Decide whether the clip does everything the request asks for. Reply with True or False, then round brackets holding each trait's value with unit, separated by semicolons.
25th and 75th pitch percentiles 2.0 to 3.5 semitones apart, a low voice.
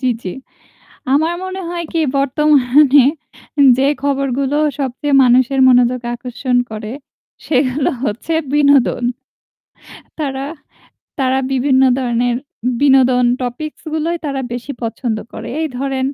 False (2.5 semitones; 265 Hz)